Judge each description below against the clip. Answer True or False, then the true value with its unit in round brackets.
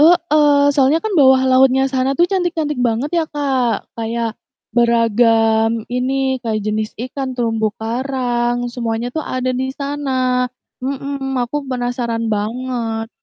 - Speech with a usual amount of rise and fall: True (3.0 semitones)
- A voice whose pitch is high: True (255 Hz)